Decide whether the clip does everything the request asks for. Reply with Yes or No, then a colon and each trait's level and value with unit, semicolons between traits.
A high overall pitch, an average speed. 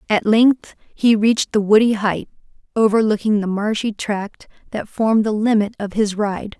Yes: high, 215 Hz; average, 165 wpm